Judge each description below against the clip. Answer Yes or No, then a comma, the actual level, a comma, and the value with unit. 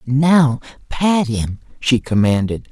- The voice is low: Yes, low, 130 Hz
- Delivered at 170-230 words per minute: No, slow, 110 wpm